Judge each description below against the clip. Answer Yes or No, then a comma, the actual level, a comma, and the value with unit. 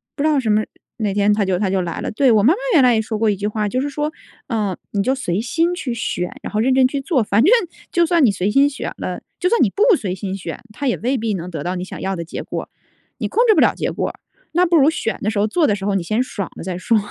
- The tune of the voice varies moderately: No, wide, 5.9 semitones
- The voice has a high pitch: Yes, high, 220 Hz